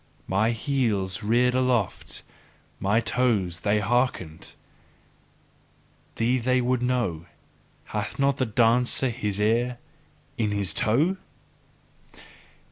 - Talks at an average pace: No, slow, 100 wpm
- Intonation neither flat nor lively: Yes, average, 3.5 semitones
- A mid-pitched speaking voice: No, low, 115 Hz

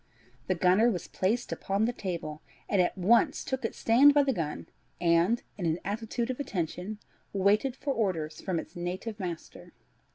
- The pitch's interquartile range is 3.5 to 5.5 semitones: Yes, average, 5.1 semitones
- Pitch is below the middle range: No, high, 200 Hz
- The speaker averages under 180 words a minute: Yes, average, 170 wpm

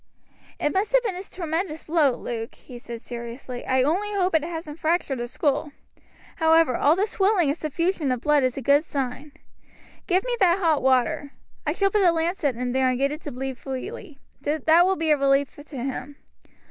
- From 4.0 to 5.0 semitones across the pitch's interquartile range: Yes, average, 4.7 semitones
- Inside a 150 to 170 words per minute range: No, average, 200 wpm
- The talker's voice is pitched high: Yes, very high, 300 Hz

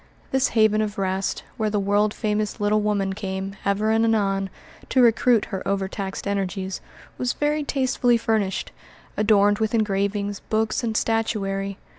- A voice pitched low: No, high, 210 Hz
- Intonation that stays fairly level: Yes, narrow, 2.1 semitones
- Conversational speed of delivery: Yes, average, 145 wpm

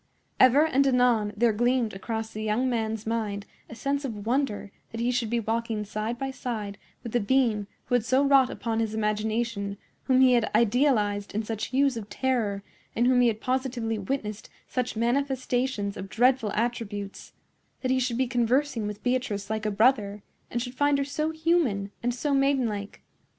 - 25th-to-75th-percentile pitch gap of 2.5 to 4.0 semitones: Yes, average, 3.4 semitones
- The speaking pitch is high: Yes, high, 235 Hz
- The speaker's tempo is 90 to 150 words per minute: No, average, 180 wpm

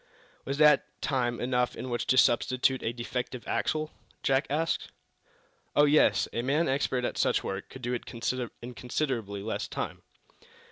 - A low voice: Yes, low, 130 Hz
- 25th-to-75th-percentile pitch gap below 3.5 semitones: Yes, average, 2.7 semitones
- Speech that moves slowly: No, average, 155 wpm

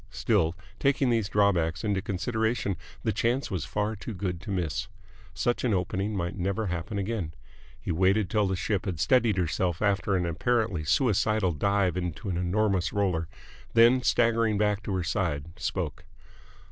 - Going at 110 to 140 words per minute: No, average, 160 wpm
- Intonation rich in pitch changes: No, average, 3.4 semitones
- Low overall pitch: Yes, low, 100 Hz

